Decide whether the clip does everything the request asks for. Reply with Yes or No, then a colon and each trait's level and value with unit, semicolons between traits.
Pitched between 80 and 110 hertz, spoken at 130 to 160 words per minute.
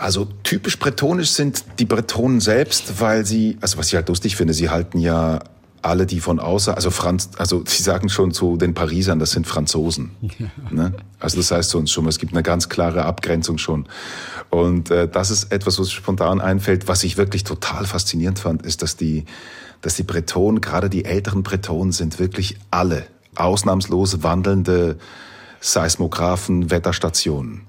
No: very low, 90 Hz; average, 175 wpm